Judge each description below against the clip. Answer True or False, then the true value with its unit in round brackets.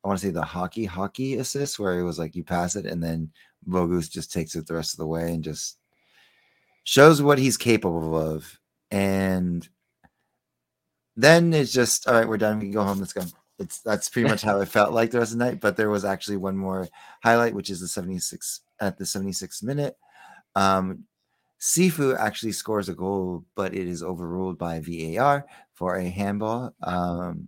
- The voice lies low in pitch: True (95 Hz)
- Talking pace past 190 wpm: True (200 wpm)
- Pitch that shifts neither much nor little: True (4.2 semitones)